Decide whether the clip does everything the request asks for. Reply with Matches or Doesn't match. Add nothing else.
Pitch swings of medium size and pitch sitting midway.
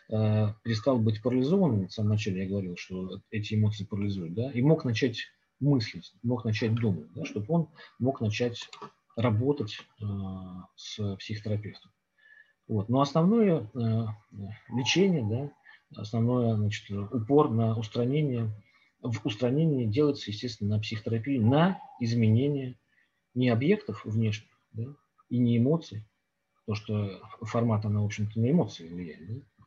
Doesn't match